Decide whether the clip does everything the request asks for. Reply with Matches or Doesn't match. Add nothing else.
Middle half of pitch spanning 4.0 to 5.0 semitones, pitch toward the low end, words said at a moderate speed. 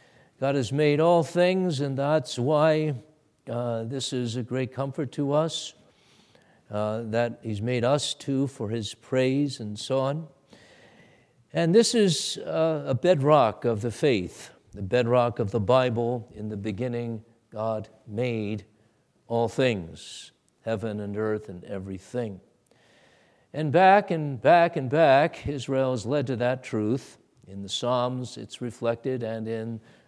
Matches